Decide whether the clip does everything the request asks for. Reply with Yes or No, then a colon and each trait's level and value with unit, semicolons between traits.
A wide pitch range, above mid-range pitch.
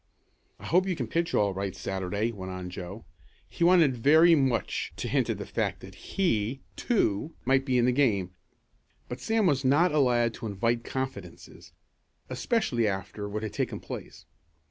No: wide, 6.3 semitones; low, 120 Hz